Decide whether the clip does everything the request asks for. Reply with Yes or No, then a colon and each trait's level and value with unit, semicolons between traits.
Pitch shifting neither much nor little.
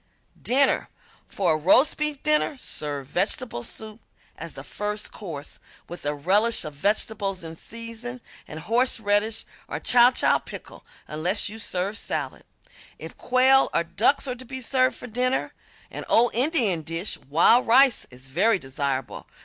No: wide, 7.1 semitones